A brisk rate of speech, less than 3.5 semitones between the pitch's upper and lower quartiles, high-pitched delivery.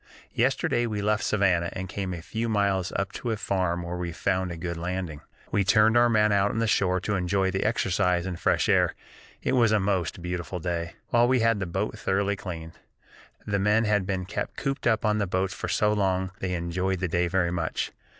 No: fast, 220 wpm; average, 3.0 semitones; very low, 95 Hz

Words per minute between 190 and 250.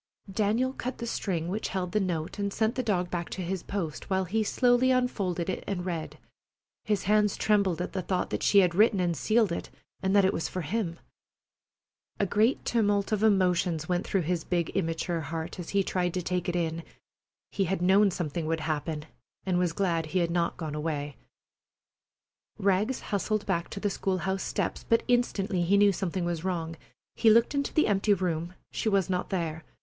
Yes: average, 200 wpm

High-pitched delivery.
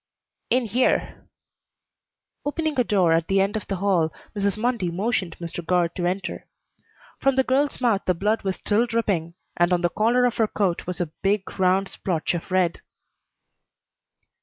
Yes: high, 195 Hz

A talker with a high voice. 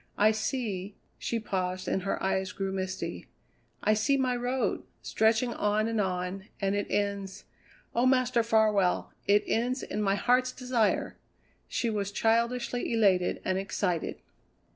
Yes: high, 210 Hz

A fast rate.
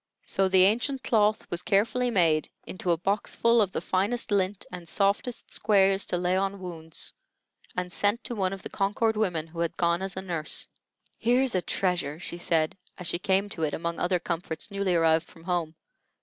No: average, 190 wpm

